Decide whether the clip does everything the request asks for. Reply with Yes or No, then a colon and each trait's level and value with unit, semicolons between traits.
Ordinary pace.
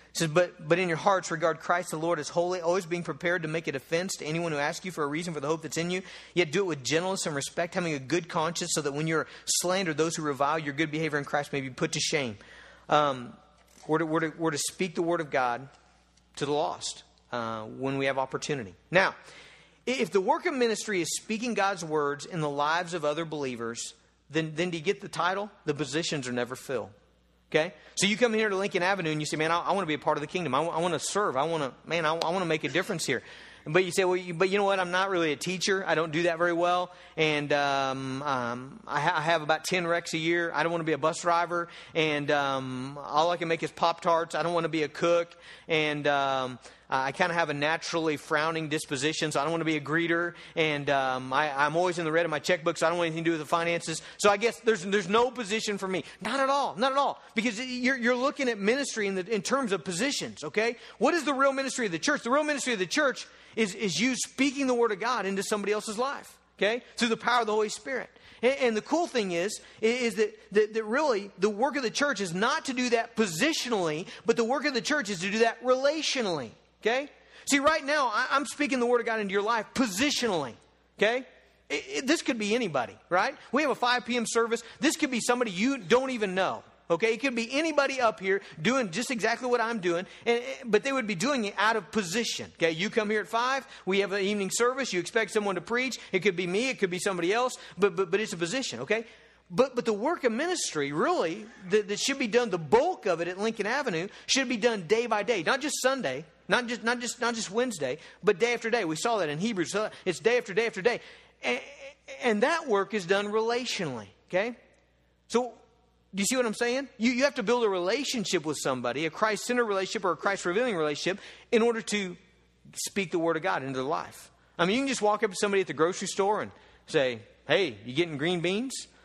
No: fast, 250 wpm